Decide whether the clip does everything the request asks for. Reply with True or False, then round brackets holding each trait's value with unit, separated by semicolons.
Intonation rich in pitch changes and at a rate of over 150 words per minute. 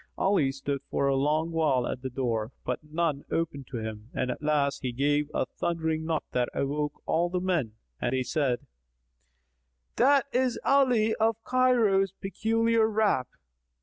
True (7.3 semitones; 160 wpm)